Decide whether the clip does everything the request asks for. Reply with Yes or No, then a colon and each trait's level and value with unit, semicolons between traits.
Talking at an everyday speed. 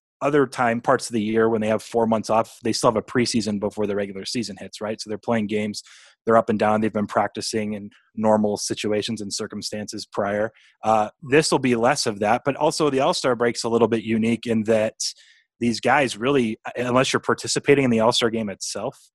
No: fast, 220 wpm